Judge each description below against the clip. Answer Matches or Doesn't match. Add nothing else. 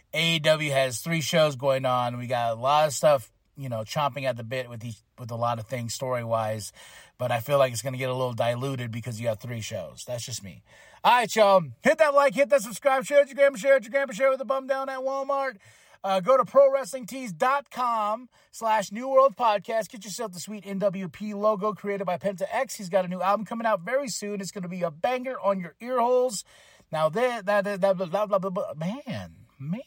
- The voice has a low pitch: Doesn't match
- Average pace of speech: Doesn't match